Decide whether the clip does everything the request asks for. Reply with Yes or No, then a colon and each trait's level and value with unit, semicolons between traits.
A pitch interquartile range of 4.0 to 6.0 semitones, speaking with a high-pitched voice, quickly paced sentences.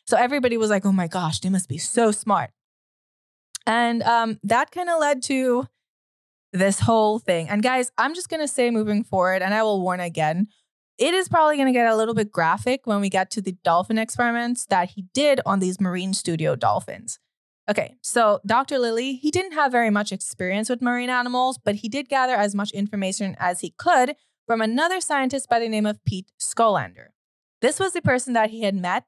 Yes: average, 4.5 semitones; high, 225 Hz; fast, 210 wpm